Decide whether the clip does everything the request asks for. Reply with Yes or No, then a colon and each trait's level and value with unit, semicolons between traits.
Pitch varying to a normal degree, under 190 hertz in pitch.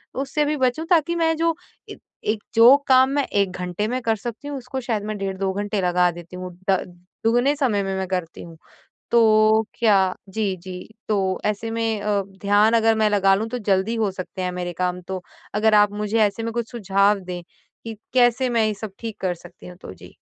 No: average, 3.5 semitones; high, 210 Hz